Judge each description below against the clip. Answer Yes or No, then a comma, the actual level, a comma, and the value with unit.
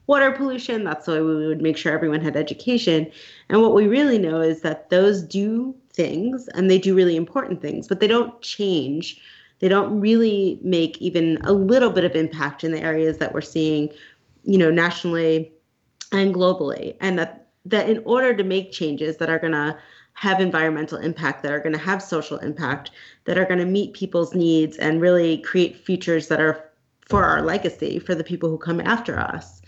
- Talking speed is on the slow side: No, average, 195 wpm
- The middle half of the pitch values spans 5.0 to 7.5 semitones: No, average, 4.0 semitones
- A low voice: No, medium, 170 Hz